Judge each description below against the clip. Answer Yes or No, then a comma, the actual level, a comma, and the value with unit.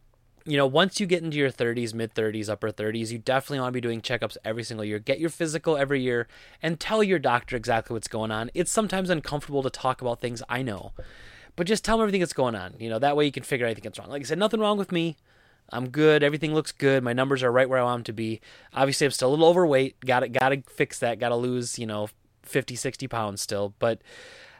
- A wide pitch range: No, average, 4.5 semitones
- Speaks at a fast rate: Yes, fast, 260 wpm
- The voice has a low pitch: Yes, low, 130 Hz